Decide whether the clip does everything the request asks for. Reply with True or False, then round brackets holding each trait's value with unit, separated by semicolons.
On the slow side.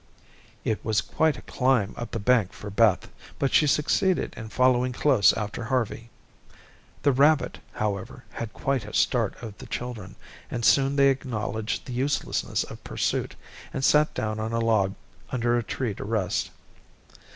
False (160 wpm)